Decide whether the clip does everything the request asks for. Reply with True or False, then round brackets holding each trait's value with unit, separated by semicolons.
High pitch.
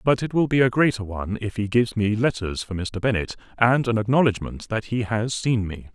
False (110 Hz)